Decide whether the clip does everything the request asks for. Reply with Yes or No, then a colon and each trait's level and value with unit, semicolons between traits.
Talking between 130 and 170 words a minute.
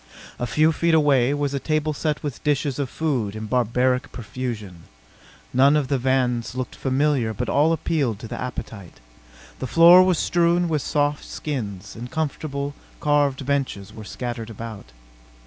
Yes: average, 160 wpm